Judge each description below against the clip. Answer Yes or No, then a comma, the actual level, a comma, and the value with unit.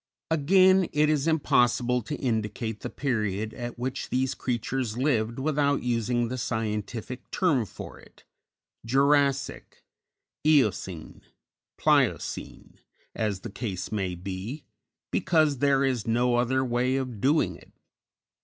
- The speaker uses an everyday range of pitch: Yes, average, 3.9 semitones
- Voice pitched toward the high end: No, low, 125 Hz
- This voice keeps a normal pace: No, slow, 125 wpm